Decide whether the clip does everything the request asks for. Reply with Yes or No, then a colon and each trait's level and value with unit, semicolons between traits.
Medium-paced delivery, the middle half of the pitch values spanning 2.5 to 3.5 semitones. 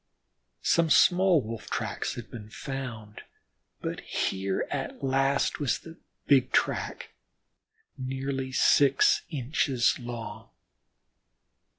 No: slow, 95 wpm; average, 2.9 semitones